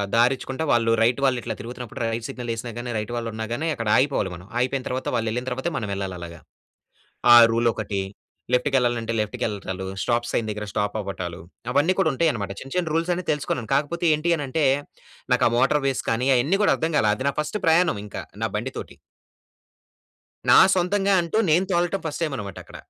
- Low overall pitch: Yes, low, 125 Hz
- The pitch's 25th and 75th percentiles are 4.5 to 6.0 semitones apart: Yes, average, 5.3 semitones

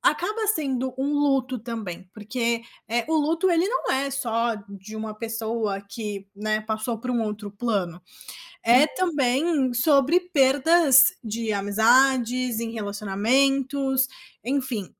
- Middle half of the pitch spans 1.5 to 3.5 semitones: No, average, 4.1 semitones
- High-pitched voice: Yes, high, 245 Hz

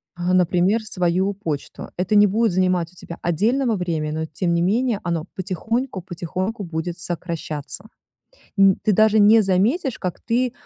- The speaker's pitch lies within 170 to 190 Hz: Yes, medium, 185 Hz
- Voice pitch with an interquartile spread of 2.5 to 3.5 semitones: No, average, 4.0 semitones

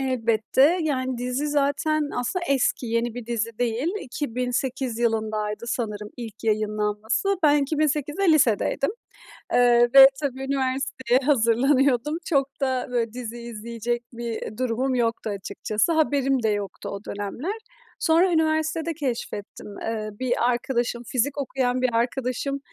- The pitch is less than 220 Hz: No, very high, 250 Hz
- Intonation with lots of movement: No, average, 3.4 semitones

